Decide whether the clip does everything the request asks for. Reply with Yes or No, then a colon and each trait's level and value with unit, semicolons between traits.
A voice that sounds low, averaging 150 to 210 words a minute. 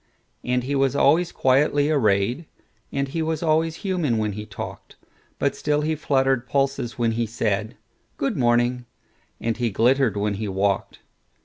No: low, 125 Hz; average, 140 wpm